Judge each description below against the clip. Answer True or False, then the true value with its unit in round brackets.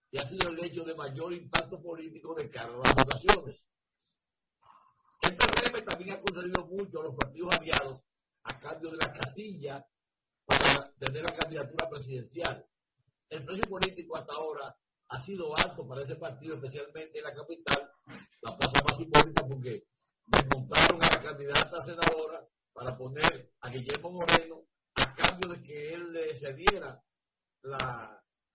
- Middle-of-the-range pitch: True (160 Hz)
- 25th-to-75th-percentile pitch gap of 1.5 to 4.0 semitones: True (3.2 semitones)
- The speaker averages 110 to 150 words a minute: True (145 wpm)